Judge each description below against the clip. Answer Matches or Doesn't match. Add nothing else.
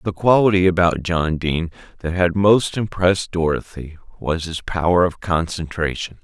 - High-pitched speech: Doesn't match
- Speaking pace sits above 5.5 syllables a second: Doesn't match